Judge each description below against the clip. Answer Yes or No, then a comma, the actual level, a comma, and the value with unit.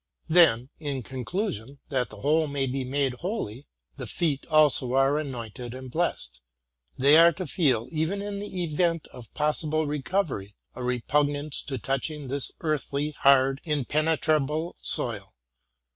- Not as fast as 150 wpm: Yes, average, 140 wpm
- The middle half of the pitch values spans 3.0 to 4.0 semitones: Yes, average, 3.3 semitones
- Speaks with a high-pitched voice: No, medium, 145 Hz